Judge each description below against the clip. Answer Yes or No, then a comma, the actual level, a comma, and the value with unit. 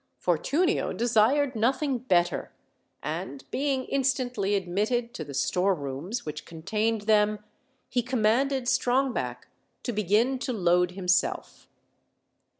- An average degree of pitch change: No, wide, 5.8 semitones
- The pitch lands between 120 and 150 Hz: No, high, 220 Hz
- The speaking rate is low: Yes, slow, 105 wpm